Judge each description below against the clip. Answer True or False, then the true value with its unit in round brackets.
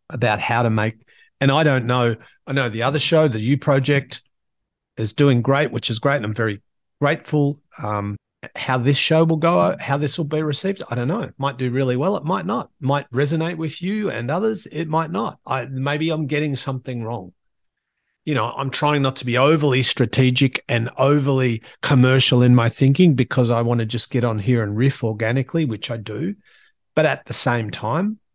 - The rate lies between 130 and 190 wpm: False (205 wpm)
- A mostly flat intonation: False (4.0 semitones)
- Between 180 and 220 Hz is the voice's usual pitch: False (135 Hz)